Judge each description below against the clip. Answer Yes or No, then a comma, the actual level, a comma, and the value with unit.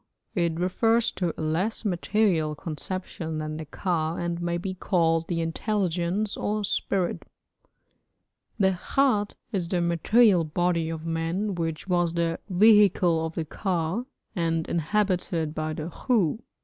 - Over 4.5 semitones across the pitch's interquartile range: No, average, 3.2 semitones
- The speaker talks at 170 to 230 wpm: No, slow, 135 wpm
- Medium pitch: Yes, medium, 175 Hz